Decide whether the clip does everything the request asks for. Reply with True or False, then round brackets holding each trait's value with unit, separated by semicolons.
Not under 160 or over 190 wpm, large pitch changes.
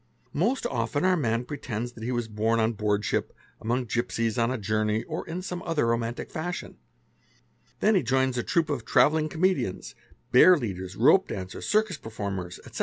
True (170 wpm; 6.1 semitones)